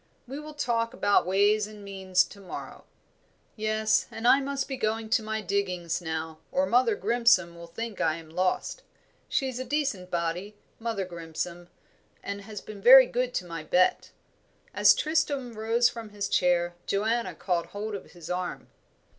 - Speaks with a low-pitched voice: No, high, 205 Hz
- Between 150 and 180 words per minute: Yes, average, 165 wpm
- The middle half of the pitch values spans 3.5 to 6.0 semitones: Yes, average, 4.6 semitones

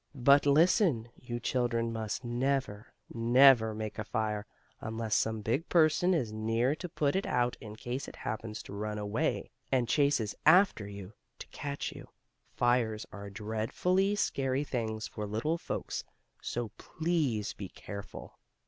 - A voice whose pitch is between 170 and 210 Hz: No, low, 115 Hz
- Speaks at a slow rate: No, average, 150 wpm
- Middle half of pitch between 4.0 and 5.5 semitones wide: Yes, average, 4.5 semitones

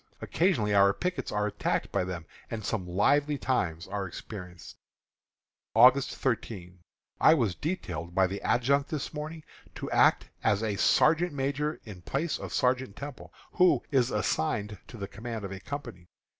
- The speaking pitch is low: Yes, low, 115 Hz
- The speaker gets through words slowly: No, average, 155 wpm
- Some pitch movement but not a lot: No, wide, 6.6 semitones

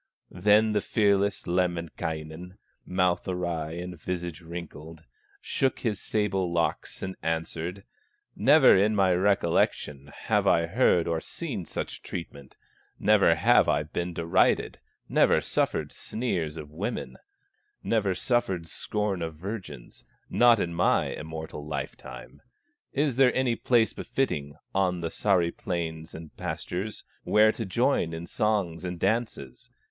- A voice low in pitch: Yes, very low, 90 Hz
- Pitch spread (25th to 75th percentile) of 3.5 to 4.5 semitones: Yes, average, 4.2 semitones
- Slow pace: Yes, slow, 130 wpm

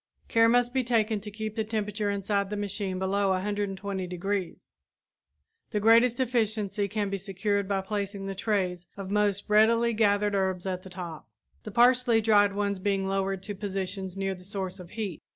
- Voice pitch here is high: Yes, high, 200 Hz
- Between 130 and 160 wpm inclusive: No, average, 175 wpm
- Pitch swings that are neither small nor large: No, narrow, 2.0 semitones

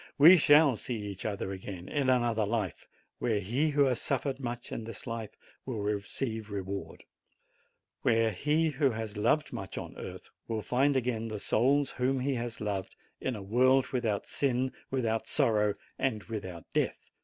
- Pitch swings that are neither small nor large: Yes, average, 3.9 semitones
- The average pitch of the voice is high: No, low, 115 Hz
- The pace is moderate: Yes, average, 165 wpm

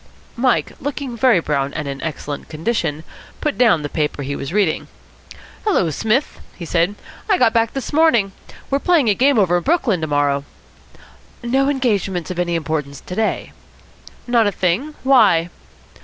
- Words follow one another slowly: No, average, 165 wpm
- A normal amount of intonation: No, wide, 8.2 semitones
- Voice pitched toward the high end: Yes, high, 195 Hz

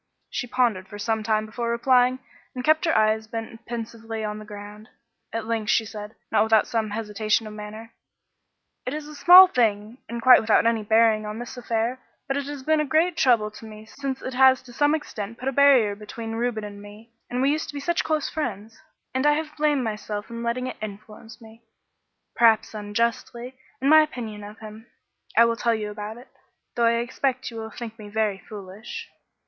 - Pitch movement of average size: Yes, average, 3.2 semitones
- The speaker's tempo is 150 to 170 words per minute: No, fast, 205 wpm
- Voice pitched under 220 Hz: No, high, 230 Hz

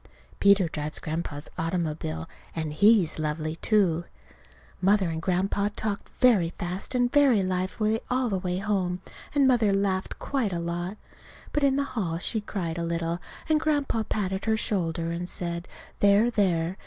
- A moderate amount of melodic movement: Yes, average, 4.2 semitones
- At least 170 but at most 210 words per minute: No, average, 155 wpm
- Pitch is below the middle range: No, medium, 185 Hz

